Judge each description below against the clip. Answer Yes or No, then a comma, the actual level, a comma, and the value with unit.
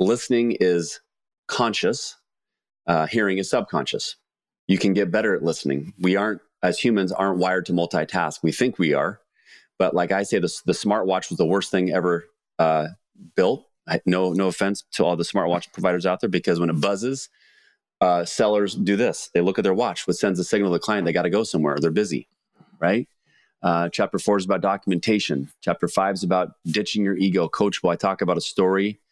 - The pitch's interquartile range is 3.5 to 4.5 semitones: No, average, 2.7 semitones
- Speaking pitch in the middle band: No, very low, 95 Hz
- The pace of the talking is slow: No, average, 200 wpm